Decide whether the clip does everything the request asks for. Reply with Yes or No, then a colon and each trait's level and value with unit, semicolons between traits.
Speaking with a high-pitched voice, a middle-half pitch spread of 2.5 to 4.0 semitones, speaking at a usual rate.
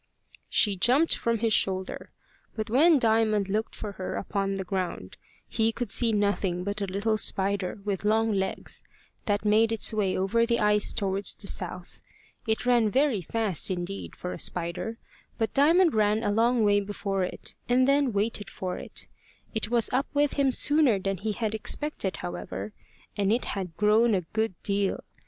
Yes: high, 210 Hz; average, 2.9 semitones; average, 175 wpm